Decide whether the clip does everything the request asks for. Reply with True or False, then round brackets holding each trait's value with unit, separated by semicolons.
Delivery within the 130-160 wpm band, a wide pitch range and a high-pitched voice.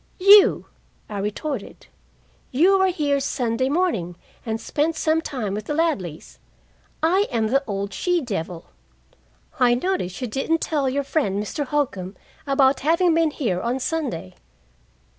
True (140 wpm; 7.2 semitones; 270 Hz)